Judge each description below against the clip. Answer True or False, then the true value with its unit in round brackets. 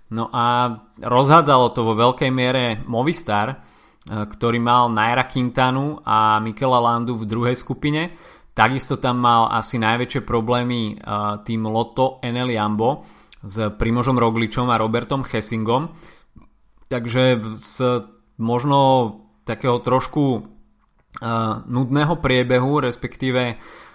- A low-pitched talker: True (120 Hz)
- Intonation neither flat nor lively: False (2.3 semitones)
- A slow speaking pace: True (105 wpm)